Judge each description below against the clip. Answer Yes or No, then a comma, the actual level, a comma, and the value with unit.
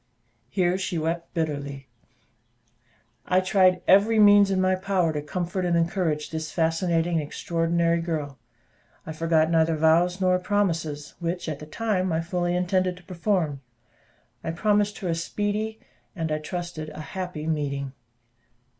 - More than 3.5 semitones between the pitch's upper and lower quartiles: No, average, 2.7 semitones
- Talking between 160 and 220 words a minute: No, average, 145 wpm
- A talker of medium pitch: Yes, medium, 170 Hz